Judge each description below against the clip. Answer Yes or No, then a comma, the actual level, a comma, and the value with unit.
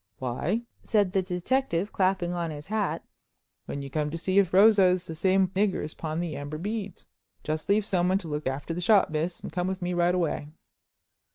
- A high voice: No, medium, 180 Hz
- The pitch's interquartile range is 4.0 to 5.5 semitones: No, average, 3.5 semitones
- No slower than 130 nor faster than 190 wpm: No, fast, 205 wpm